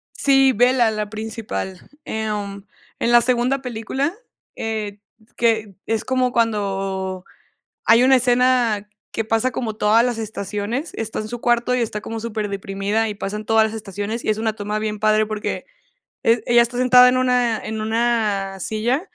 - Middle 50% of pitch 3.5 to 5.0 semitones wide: No, narrow, 2.4 semitones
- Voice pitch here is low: No, high, 220 Hz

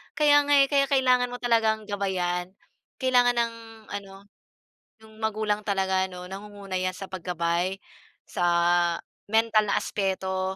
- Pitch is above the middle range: Yes, high, 205 Hz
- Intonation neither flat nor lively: Yes, average, 3.7 semitones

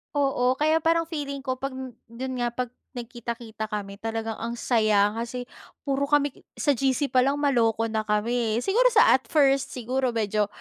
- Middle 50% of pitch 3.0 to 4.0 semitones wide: Yes, average, 3.7 semitones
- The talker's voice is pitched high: Yes, very high, 250 Hz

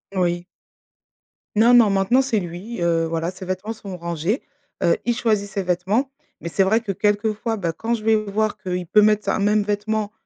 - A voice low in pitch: No, high, 205 Hz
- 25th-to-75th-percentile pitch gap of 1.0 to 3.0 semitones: No, average, 3.4 semitones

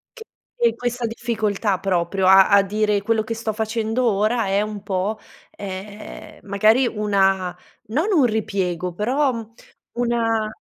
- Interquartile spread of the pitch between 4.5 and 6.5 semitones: No, average, 2.7 semitones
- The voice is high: Yes, high, 215 Hz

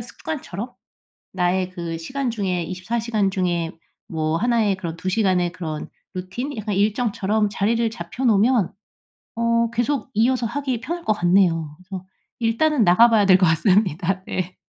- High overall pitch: Yes, high, 200 Hz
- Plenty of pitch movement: No, average, 4.4 semitones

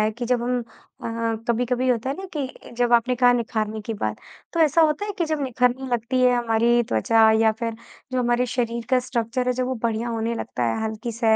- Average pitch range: No, narrow, 1.9 semitones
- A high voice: Yes, high, 240 Hz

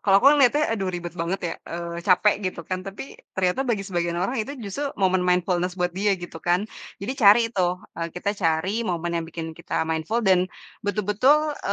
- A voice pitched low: No, medium, 185 Hz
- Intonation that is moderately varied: Yes, average, 3.2 semitones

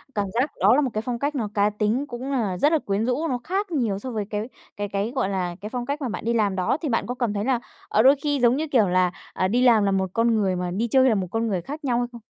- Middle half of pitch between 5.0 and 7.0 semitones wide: No, average, 4.3 semitones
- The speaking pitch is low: No, high, 230 Hz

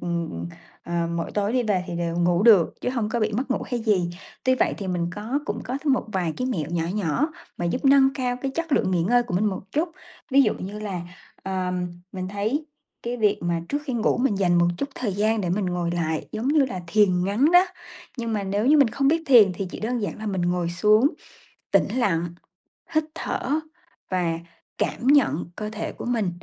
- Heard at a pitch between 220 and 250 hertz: No, high, 210 Hz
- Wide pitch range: Yes, wide, 5.9 semitones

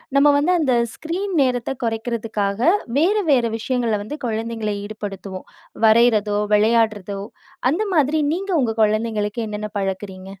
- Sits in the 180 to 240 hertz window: Yes, high, 225 Hz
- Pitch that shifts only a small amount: No, average, 3.7 semitones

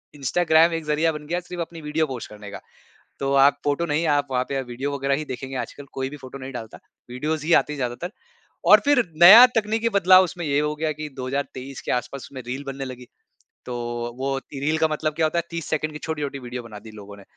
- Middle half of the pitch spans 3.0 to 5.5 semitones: Yes, average, 3.3 semitones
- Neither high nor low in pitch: Yes, medium, 145 Hz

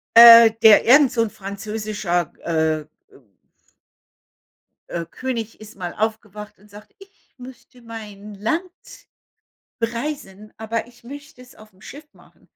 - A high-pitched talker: Yes, high, 220 Hz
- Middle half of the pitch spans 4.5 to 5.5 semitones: No, average, 3.2 semitones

